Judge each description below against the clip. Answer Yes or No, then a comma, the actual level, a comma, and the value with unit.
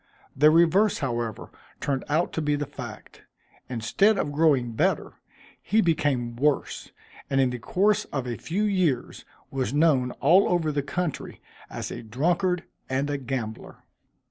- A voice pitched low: No, medium, 145 Hz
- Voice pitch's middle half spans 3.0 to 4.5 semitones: No, average, 5.2 semitones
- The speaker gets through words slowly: No, average, 150 wpm